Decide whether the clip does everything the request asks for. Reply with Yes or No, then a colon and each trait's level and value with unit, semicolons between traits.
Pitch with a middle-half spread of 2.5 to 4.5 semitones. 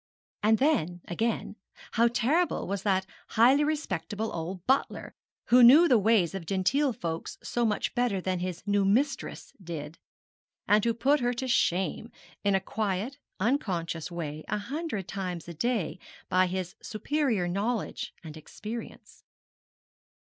No: average, 5.1 semitones